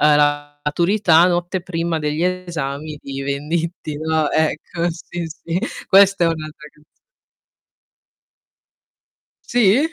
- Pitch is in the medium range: Yes, medium, 160 Hz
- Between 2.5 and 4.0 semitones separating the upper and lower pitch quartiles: Yes, average, 2.8 semitones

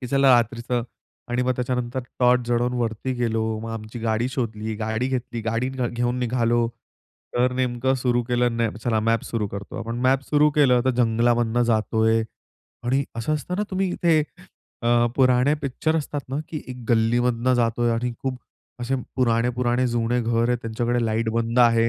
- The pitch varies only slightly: Yes, narrow, 1.7 semitones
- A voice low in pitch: Yes, low, 120 Hz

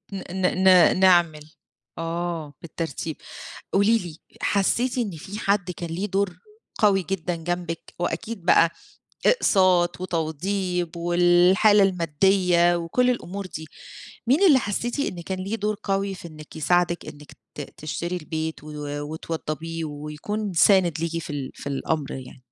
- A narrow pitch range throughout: No, average, 3.3 semitones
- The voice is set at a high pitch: No, medium, 175 Hz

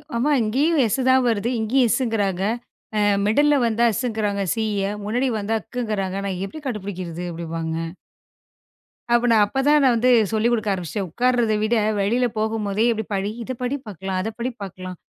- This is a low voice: No, high, 220 Hz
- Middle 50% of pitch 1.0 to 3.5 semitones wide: No, average, 3.9 semitones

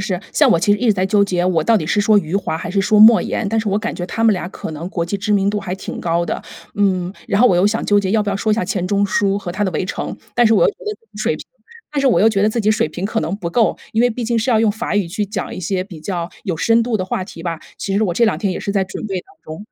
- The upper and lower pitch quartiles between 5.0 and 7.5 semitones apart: No, average, 2.9 semitones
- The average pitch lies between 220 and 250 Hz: No, high, 200 Hz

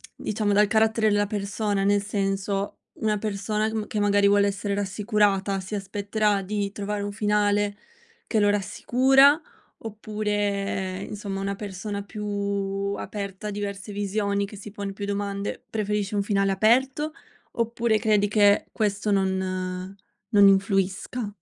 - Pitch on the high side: Yes, high, 205 Hz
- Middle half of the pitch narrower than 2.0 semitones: Yes, narrow, 1.1 semitones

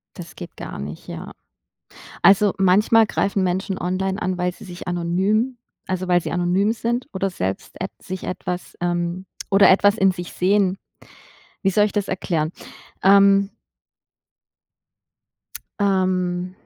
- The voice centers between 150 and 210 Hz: Yes, medium, 185 Hz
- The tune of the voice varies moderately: No, narrow, 1.9 semitones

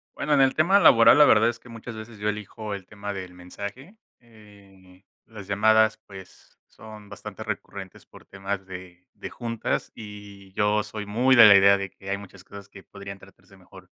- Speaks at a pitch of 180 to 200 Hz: No, low, 105 Hz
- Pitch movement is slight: Yes, narrow, 2.2 semitones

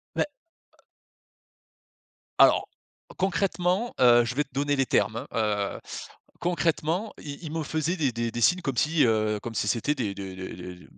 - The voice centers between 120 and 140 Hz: Yes, low, 135 Hz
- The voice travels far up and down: Yes, wide, 6.9 semitones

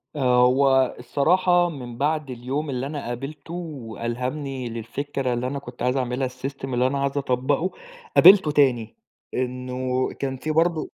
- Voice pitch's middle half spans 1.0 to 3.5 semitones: Yes, average, 2.8 semitones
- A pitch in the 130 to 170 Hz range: Yes, low, 135 Hz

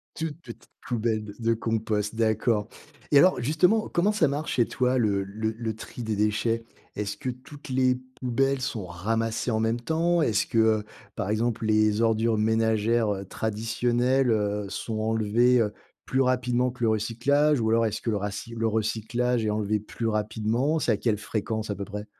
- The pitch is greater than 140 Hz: No, low, 115 Hz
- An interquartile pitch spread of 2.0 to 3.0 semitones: Yes, narrow, 2.5 semitones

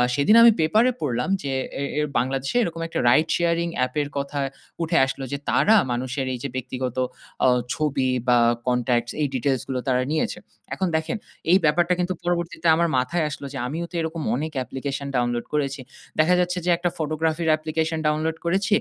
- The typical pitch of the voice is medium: Yes, medium, 155 Hz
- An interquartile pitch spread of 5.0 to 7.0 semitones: No, average, 4.2 semitones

